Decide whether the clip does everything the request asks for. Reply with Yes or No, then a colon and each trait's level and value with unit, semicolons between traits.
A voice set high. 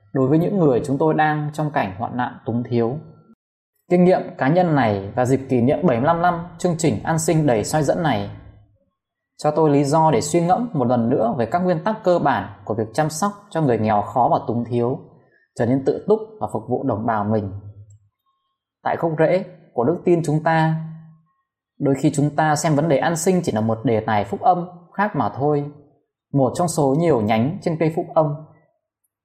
No: medium, 150 Hz